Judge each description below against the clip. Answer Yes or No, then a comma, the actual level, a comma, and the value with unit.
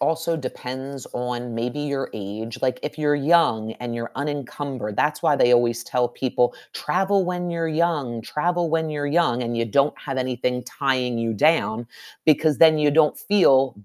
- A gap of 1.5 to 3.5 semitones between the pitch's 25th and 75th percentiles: No, average, 4.4 semitones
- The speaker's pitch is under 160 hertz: Yes, low, 135 Hz